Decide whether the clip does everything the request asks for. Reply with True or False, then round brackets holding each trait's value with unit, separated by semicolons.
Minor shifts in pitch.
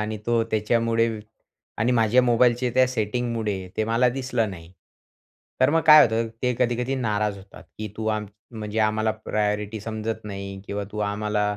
True (2.3 semitones)